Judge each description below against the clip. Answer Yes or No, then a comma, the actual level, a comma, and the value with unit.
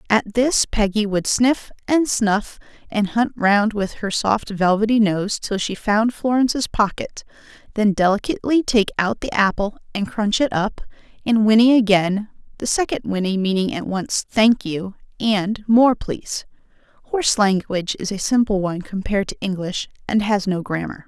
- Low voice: No, high, 210 Hz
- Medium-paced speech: Yes, average, 160 wpm